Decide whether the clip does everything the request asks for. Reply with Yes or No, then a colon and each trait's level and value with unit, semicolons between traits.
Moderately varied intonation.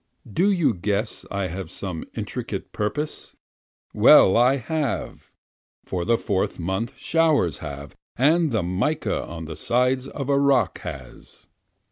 No: wide, 7.2 semitones